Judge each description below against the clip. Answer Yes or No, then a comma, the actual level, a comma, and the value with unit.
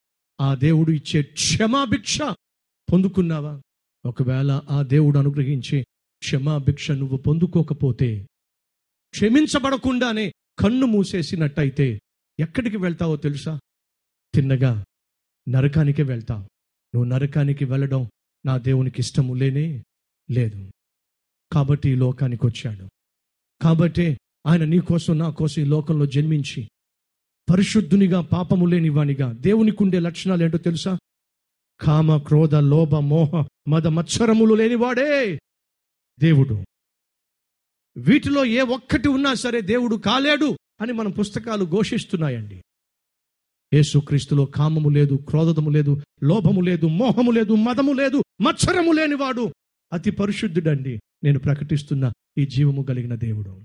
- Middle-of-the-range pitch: Yes, medium, 155 Hz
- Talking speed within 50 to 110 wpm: Yes, average, 100 wpm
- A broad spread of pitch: Yes, wide, 5.7 semitones